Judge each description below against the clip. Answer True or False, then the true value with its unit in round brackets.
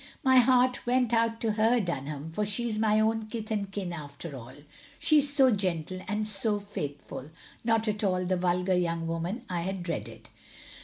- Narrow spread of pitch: False (4.7 semitones)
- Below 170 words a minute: False (190 wpm)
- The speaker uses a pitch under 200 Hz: False (205 Hz)